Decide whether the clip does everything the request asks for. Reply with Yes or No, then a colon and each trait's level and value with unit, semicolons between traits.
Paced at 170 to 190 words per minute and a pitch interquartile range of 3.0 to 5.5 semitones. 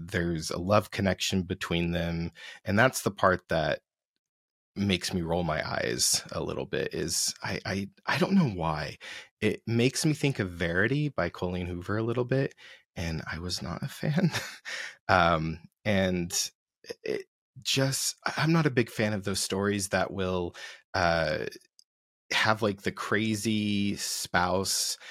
No: average, 155 wpm; average, 4.8 semitones